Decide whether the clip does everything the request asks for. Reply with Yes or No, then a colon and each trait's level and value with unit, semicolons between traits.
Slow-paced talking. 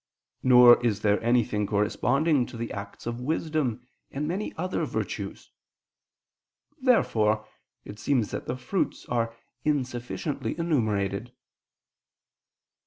Yes: slow, 110 wpm